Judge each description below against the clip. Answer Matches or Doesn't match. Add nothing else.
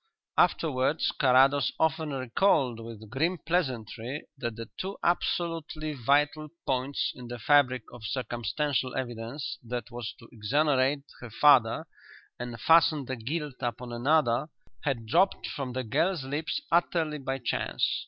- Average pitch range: Matches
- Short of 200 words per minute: Matches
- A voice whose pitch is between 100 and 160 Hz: Matches